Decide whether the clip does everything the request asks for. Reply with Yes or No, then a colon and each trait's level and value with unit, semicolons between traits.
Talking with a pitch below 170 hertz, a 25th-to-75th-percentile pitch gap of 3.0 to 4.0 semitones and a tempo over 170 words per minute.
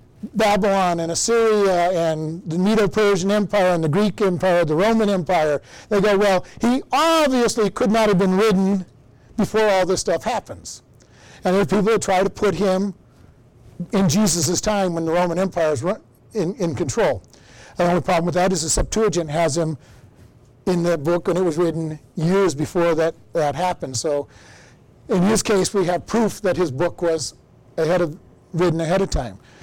No: medium, 180 Hz; average, 3.7 semitones; average, 180 wpm